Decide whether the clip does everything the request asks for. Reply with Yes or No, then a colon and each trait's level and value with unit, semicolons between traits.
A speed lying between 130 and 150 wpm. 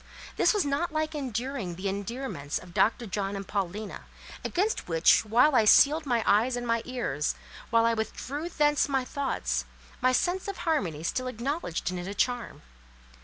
No: average, 170 wpm